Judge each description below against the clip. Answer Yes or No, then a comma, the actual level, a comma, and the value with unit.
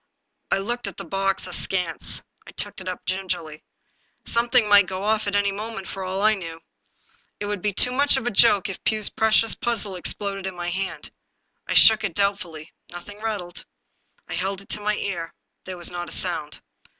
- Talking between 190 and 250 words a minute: Yes, average, 195 wpm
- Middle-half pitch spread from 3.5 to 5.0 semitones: No, average, 2.7 semitones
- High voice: Yes, high, 195 Hz